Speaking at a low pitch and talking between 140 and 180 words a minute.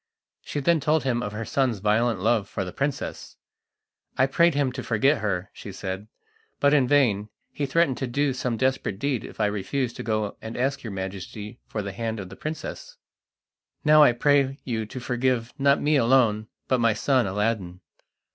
No: low, 120 Hz; average, 190 wpm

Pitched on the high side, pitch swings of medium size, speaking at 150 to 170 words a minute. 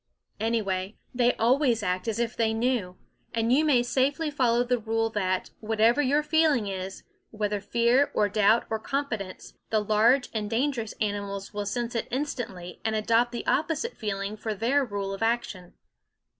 Yes: high, 225 Hz; average, 3.3 semitones; average, 165 wpm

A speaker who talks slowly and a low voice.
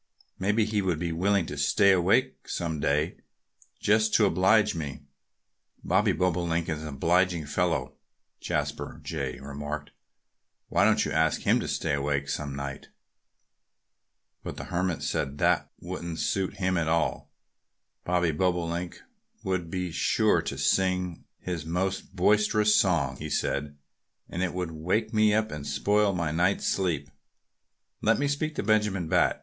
No: average, 155 wpm; very low, 90 Hz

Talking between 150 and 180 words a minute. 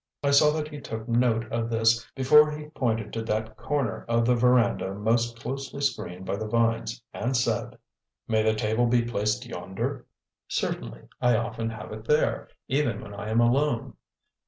Yes: average, 175 wpm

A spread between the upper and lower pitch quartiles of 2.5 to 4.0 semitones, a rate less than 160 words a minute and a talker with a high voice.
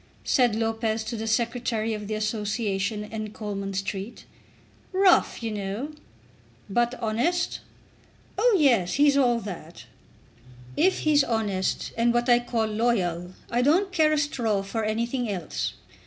Yes: average, 2.9 semitones; average, 140 wpm; high, 225 Hz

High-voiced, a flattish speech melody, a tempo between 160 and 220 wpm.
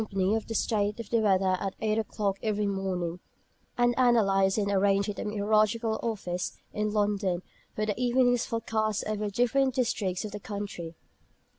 Yes: high, 210 Hz; narrow, 2.3 semitones; average, 165 wpm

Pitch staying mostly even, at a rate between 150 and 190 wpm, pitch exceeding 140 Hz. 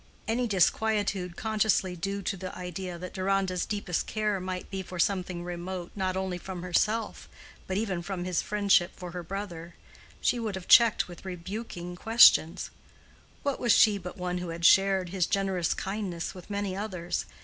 Yes: narrow, 2.3 semitones; average, 165 wpm; high, 190 Hz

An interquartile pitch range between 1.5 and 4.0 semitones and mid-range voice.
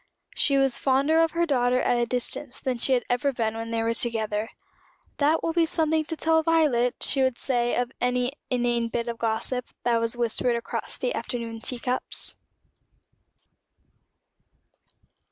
No: average, 3.1 semitones; high, 245 Hz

